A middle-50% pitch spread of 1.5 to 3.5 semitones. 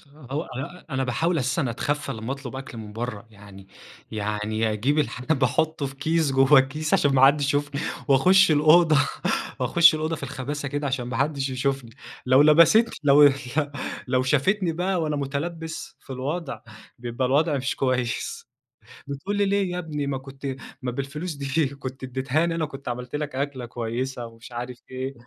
Yes: average, 3.2 semitones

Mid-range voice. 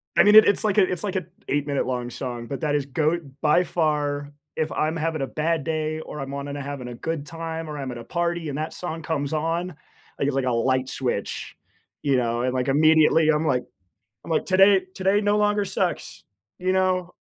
Yes: medium, 155 Hz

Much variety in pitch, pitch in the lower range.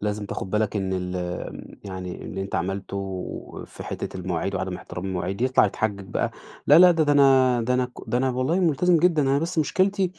Yes: wide, 7.4 semitones; low, 110 Hz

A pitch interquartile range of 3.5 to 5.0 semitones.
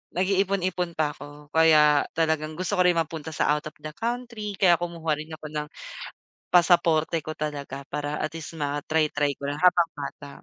No: average, 2.8 semitones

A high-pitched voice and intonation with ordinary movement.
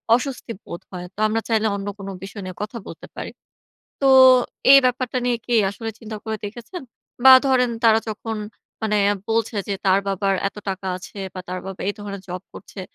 Yes: high, 215 Hz; average, 3.3 semitones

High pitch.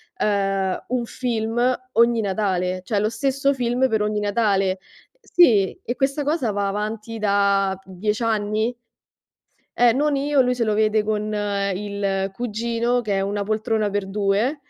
Yes: high, 215 Hz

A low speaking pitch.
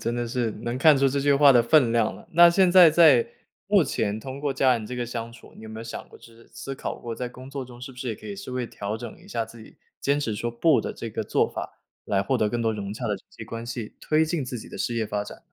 Yes: low, 120 Hz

